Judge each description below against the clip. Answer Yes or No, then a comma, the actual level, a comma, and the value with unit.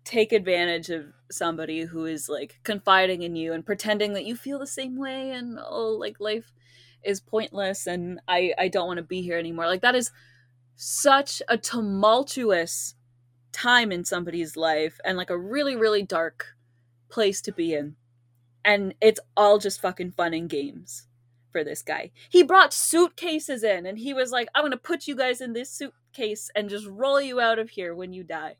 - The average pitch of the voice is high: Yes, high, 195 Hz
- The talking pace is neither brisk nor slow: Yes, average, 190 wpm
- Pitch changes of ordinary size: No, wide, 6.3 semitones